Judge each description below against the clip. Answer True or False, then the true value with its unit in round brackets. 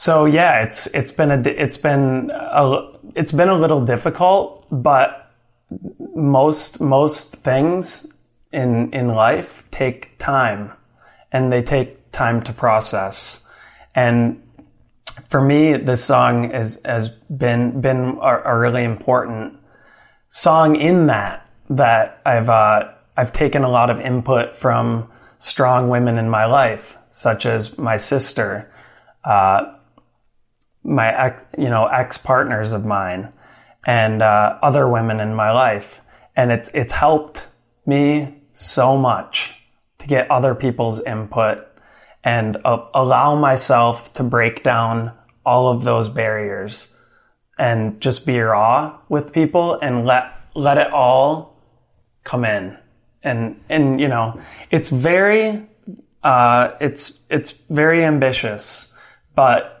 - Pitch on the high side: False (125 Hz)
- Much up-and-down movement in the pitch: False (3.9 semitones)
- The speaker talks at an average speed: False (125 wpm)